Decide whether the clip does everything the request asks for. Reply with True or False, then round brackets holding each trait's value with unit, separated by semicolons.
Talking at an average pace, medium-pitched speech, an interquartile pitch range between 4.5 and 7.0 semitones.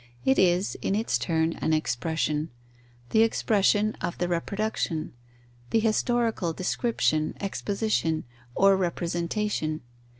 False (105 wpm; 180 Hz; 4.9 semitones)